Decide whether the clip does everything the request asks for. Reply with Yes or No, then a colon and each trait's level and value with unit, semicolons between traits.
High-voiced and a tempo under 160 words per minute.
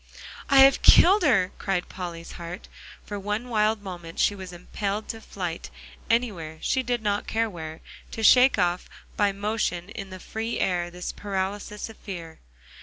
No: high, 200 Hz; average, 165 wpm